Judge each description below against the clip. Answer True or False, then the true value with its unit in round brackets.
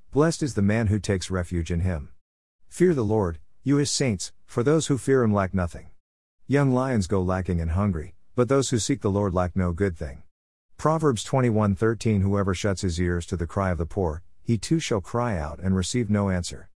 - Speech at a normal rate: False (210 wpm)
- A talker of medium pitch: False (100 Hz)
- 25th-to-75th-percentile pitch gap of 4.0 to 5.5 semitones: True (5.2 semitones)